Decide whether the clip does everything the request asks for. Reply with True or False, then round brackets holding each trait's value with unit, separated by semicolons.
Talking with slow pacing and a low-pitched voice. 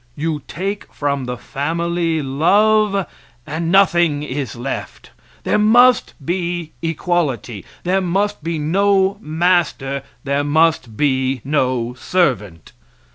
False (110 wpm; 160 Hz)